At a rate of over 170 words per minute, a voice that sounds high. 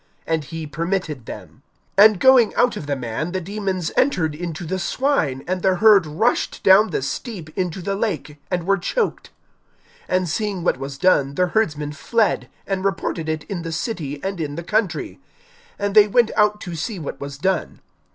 No: average, 185 wpm; medium, 180 Hz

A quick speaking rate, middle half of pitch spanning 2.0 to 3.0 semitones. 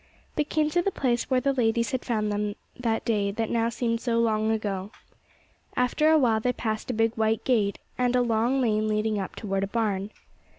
Yes: fast, 210 wpm; narrow, 2.6 semitones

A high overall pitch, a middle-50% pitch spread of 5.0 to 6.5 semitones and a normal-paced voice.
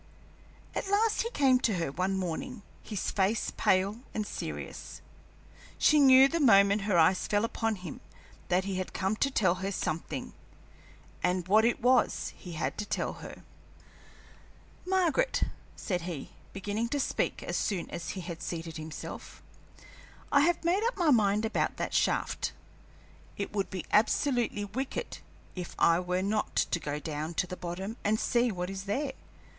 Yes: high, 200 Hz; wide, 5.5 semitones; average, 160 wpm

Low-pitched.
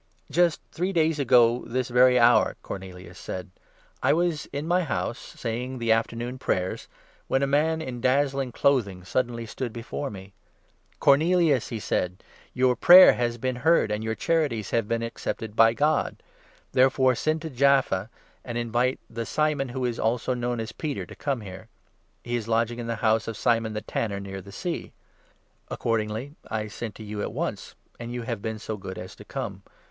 Yes: low, 120 Hz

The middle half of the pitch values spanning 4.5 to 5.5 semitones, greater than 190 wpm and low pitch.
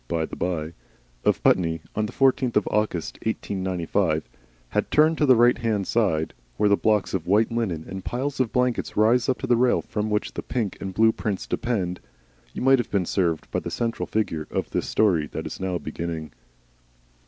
Yes: average, 5.1 semitones; average, 200 wpm; low, 105 Hz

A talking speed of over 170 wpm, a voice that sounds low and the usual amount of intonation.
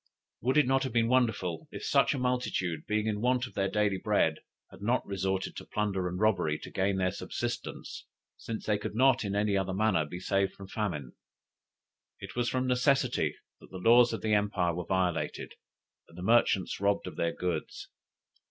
Yes: average, 190 wpm; low, 100 Hz; average, 4.1 semitones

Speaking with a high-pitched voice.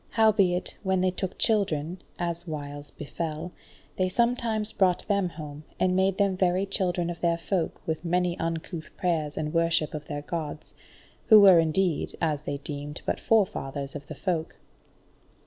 No: medium, 170 Hz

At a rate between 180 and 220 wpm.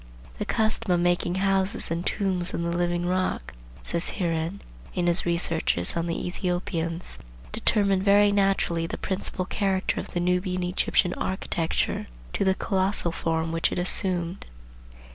No: average, 145 wpm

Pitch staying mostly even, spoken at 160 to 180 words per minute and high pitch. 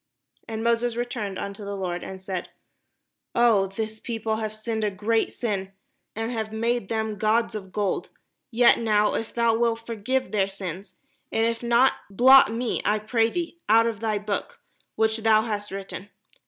Yes: narrow, 2.2 semitones; average, 175 wpm; high, 220 Hz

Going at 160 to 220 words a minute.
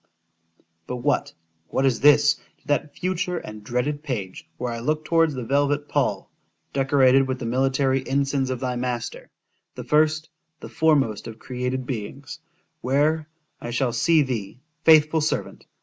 No: average, 140 wpm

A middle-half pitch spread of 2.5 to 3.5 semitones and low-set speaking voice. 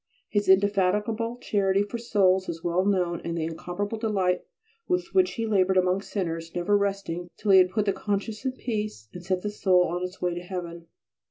No: average, 2.8 semitones; high, 190 Hz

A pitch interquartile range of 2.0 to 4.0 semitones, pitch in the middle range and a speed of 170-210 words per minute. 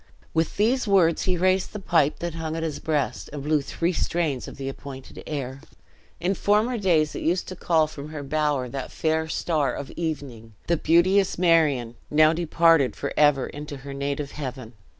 Yes: average, 3.4 semitones; medium, 155 Hz; average, 185 wpm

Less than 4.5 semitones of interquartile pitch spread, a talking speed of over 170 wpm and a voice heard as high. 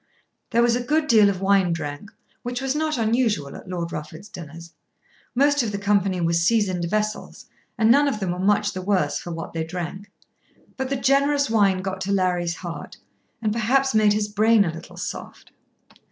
No: average, 4.8 semitones; average, 190 wpm; high, 205 Hz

